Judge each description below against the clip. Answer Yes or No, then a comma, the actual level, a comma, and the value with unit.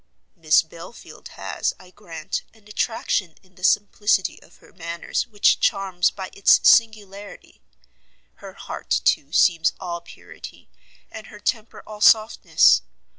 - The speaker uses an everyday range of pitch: Yes, average, 3.4 semitones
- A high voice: Yes, high, 195 Hz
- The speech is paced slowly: Yes, slow, 130 wpm